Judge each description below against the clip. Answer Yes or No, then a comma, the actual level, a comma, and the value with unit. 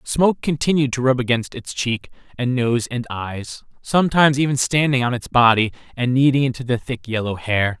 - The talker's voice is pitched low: Yes, low, 125 Hz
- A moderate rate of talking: Yes, average, 185 wpm